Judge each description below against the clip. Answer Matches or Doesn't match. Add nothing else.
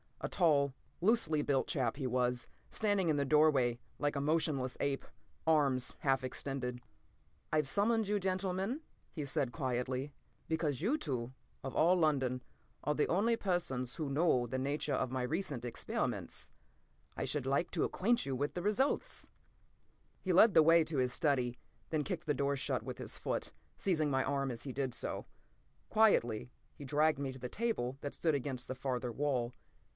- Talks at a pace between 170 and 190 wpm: Matches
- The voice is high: Doesn't match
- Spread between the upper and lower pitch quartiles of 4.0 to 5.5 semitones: Matches